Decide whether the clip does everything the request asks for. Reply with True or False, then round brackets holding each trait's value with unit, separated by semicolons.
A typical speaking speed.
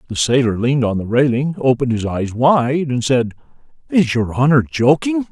True (180 wpm)